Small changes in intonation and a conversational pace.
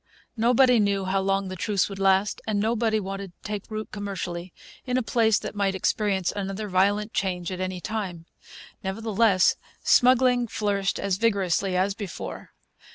Yes: narrow, 2.3 semitones; average, 160 wpm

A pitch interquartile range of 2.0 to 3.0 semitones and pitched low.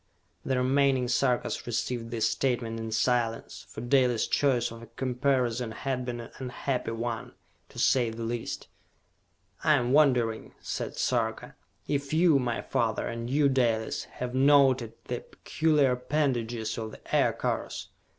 Yes: narrow, 2.6 semitones; low, 125 Hz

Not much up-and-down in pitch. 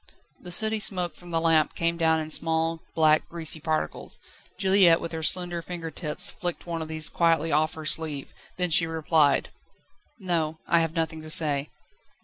Yes: narrow, 1.5 semitones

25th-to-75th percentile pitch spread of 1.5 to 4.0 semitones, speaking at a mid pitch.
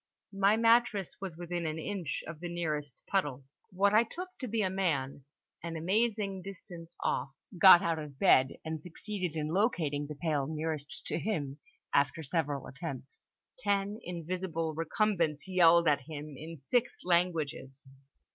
No: average, 4.4 semitones; medium, 165 Hz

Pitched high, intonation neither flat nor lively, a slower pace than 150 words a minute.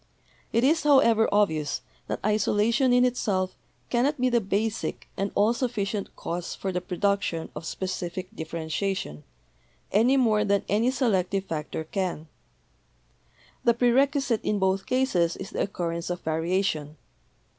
Yes: high, 200 Hz; average, 5.0 semitones; average, 140 wpm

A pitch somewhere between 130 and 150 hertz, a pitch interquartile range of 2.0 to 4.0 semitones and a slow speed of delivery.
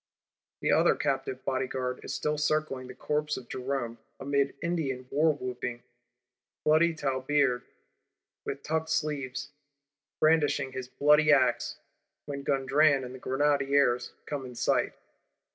Yes: medium, 140 Hz; narrow, 2.6 semitones; slow, 125 wpm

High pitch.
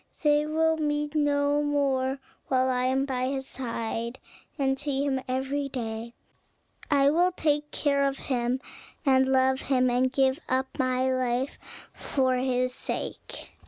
Yes: very high, 265 Hz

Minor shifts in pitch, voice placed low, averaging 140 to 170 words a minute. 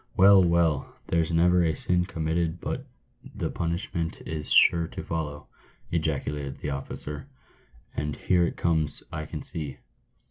Yes: narrow, 2.3 semitones; very low, 80 Hz; average, 150 wpm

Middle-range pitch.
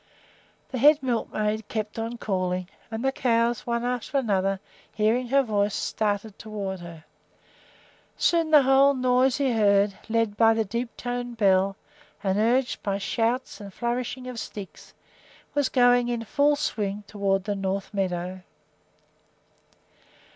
No: high, 225 Hz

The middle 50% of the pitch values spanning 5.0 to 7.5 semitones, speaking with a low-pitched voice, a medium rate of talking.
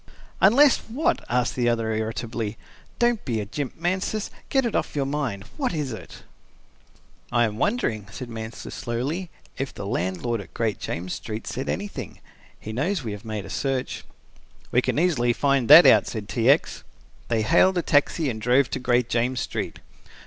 Yes: wide, 5.4 semitones; low, 125 Hz; average, 180 wpm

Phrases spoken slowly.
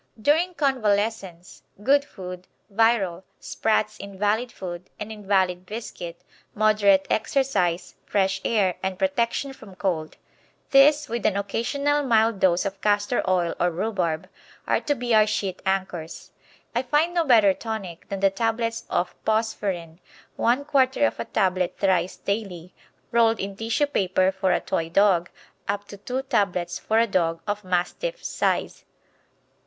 No: average, 145 wpm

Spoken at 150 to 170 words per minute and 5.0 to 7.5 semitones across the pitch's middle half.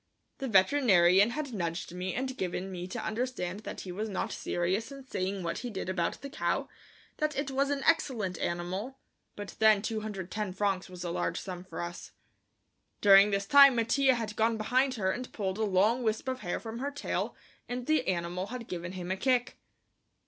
No: average, 190 wpm; average, 5.3 semitones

